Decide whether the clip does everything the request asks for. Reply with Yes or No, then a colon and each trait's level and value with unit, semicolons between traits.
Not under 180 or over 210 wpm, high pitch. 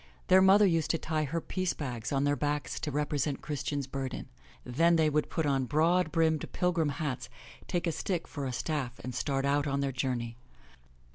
No: average, 195 wpm; medium, 145 Hz